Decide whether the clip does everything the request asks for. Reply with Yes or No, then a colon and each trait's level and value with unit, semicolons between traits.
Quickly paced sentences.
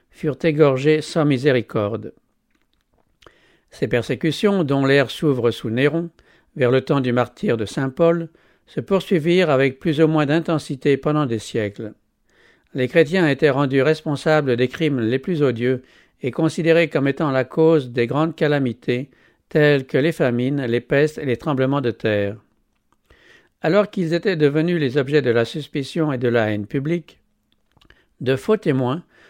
No: average, 155 wpm